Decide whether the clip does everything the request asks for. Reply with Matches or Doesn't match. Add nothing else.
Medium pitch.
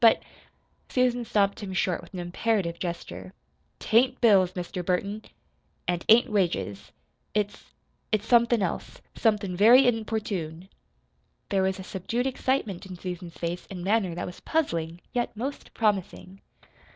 Doesn't match